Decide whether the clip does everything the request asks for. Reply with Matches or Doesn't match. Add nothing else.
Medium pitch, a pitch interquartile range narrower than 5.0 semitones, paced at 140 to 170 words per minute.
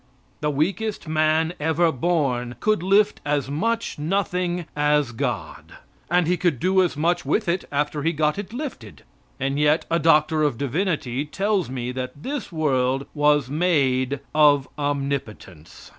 Matches